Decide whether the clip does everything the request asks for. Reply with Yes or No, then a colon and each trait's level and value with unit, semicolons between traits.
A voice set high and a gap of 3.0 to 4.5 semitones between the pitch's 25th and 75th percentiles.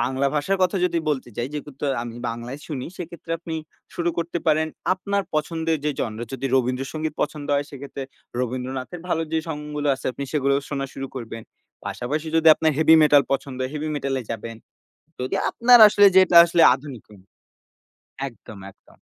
No: medium, 145 Hz; average, 3.9 semitones